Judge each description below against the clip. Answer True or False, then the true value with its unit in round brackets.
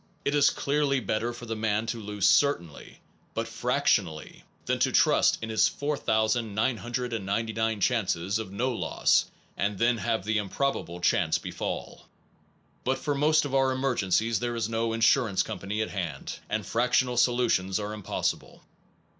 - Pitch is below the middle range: True (115 Hz)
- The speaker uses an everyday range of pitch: True (3.3 semitones)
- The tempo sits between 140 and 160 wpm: True (150 wpm)